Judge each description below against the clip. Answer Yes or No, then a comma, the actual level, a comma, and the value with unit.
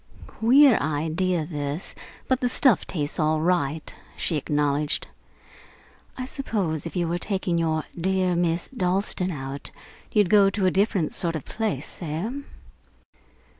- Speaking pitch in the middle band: Yes, medium, 175 Hz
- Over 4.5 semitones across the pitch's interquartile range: No, average, 4.1 semitones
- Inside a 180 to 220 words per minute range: No, slow, 135 wpm